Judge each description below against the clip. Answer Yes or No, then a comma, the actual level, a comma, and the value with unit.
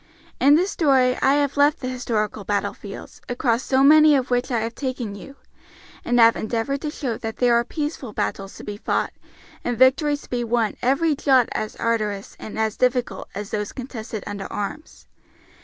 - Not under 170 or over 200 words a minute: Yes, average, 185 wpm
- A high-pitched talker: Yes, high, 245 Hz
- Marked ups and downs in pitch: No, average, 3.9 semitones